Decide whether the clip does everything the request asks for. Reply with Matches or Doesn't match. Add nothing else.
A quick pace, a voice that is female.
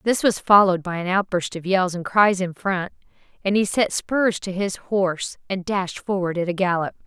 Matches